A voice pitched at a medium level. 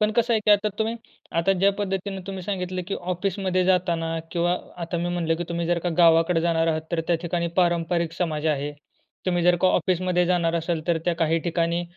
Yes: medium, 175 Hz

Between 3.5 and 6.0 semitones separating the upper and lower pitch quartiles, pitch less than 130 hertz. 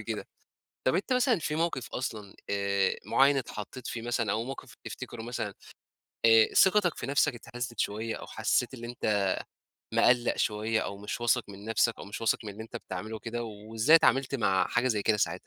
No: average, 3.1 semitones; low, 115 Hz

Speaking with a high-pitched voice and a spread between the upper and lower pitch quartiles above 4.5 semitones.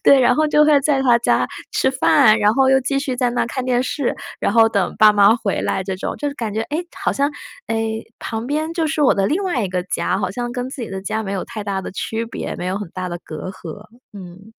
Yes: high, 225 Hz; average, 5.0 semitones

